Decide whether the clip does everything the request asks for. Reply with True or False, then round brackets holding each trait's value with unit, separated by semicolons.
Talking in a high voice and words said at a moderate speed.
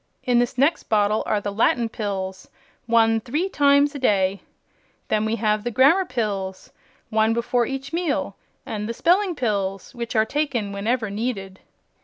True (225 Hz; 160 wpm)